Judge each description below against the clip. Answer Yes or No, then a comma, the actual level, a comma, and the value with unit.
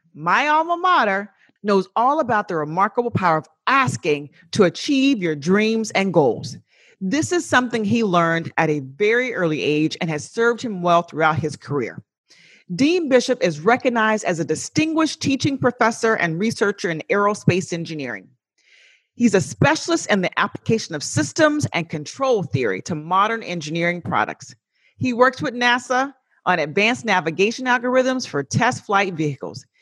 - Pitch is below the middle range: No, high, 200 Hz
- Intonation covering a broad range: Yes, wide, 7.1 semitones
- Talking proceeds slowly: No, average, 155 wpm